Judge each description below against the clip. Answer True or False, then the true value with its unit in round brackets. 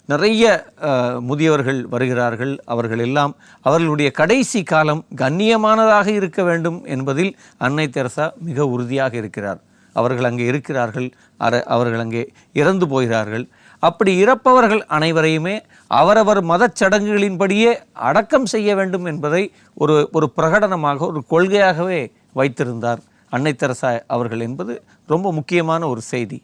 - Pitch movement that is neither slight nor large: False (7.5 semitones)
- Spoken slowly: False (110 wpm)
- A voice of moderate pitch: True (155 Hz)